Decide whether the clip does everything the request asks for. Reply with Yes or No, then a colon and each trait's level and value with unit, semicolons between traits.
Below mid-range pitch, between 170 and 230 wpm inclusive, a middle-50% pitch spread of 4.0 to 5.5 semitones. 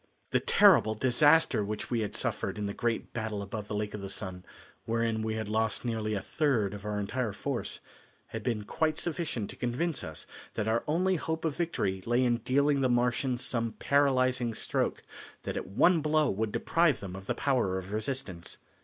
Yes: low, 115 Hz; average, 195 wpm; average, 4.8 semitones